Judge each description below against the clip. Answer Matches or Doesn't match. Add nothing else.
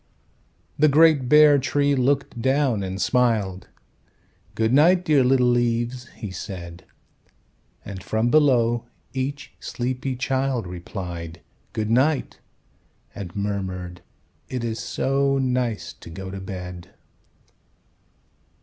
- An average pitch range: Doesn't match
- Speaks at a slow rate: Matches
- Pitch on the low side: Matches